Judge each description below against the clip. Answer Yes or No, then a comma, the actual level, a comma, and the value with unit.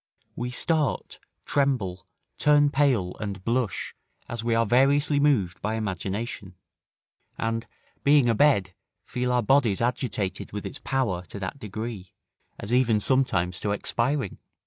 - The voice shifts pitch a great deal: No, average, 5.0 semitones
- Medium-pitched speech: No, low, 115 Hz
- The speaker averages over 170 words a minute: No, slow, 135 wpm